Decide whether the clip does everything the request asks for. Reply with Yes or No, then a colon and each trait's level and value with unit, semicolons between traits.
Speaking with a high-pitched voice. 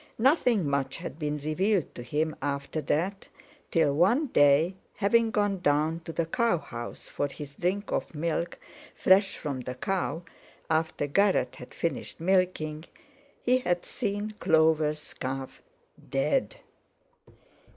No: medium, 165 Hz